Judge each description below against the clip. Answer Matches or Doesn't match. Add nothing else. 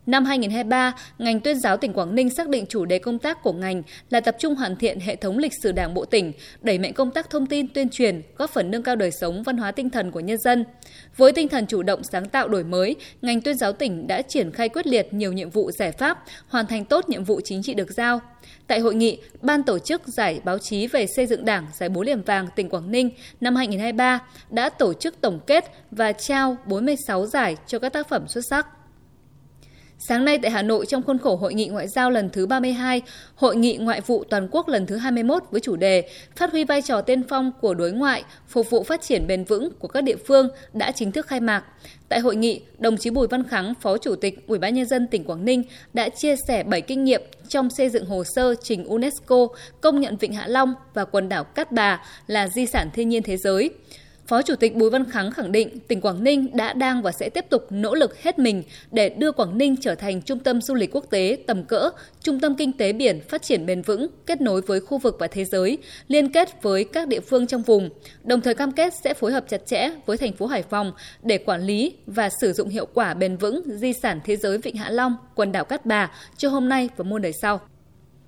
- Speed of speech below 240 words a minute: Doesn't match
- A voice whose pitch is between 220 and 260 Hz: Matches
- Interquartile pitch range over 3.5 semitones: Matches